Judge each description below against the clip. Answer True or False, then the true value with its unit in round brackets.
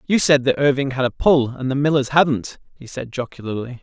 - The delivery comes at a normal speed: False (220 wpm)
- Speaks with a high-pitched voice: False (135 Hz)